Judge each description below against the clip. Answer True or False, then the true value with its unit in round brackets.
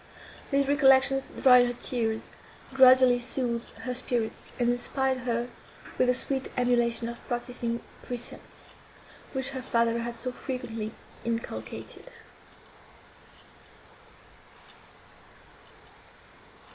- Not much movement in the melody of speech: True (1.8 semitones)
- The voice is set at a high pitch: True (245 Hz)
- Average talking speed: False (95 wpm)